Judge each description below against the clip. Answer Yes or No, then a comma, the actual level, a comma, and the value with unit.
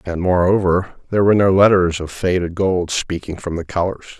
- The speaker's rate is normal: Yes, average, 185 wpm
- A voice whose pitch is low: Yes, very low, 90 Hz